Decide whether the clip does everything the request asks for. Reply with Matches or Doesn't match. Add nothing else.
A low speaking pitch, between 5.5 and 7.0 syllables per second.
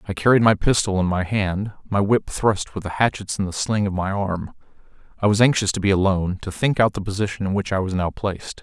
Matches